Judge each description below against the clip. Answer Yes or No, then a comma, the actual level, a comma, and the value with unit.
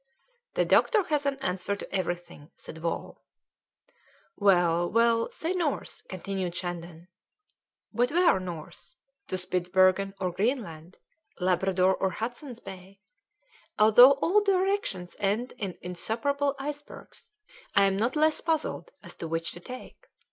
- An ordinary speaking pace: No, slow, 125 wpm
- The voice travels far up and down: Yes, wide, 7.3 semitones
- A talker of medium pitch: No, high, 195 Hz